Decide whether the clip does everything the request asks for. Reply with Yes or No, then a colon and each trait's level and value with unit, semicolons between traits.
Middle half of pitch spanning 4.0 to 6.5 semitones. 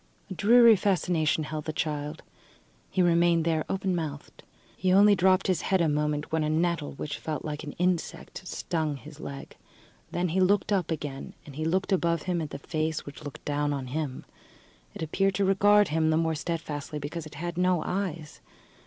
No: average, 3.4 semitones